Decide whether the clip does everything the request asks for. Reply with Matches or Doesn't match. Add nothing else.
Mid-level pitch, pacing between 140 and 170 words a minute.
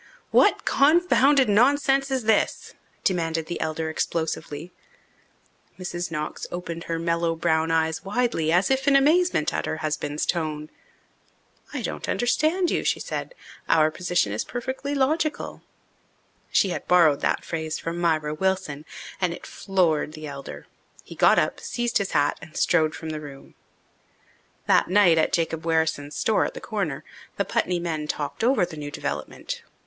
Matches